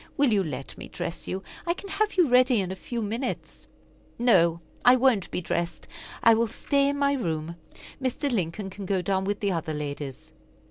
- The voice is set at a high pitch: Yes, high, 205 Hz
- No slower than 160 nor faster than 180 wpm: No, average, 195 wpm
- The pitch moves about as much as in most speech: No, wide, 6.8 semitones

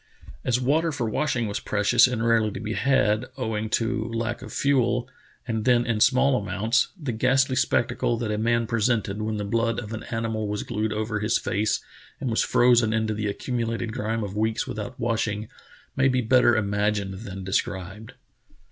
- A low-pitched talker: Yes, low, 115 Hz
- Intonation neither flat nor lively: No, narrow, 2.3 semitones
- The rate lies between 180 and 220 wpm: Yes, average, 185 wpm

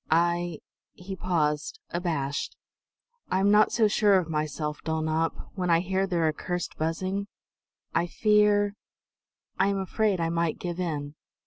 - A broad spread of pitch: No, average, 3.3 semitones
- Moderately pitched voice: Yes, medium, 175 Hz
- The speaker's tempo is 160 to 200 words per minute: No, average, 140 wpm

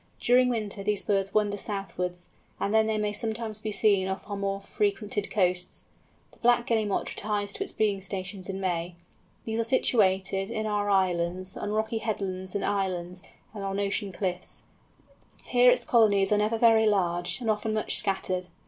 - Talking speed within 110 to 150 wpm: No, average, 175 wpm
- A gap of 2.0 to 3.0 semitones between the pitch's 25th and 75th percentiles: Yes, narrow, 2.4 semitones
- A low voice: No, high, 205 Hz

